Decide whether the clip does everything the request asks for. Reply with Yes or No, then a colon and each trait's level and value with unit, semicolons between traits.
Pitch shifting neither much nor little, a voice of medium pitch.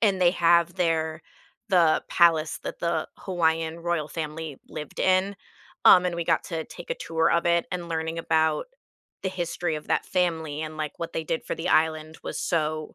No: narrow, 1.5 semitones; medium, 165 Hz